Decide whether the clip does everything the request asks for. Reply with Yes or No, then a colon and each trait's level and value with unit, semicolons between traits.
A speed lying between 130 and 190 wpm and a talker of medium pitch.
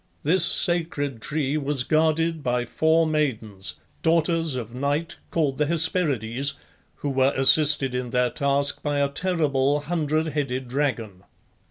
Yes: slow, 135 wpm; medium, 145 Hz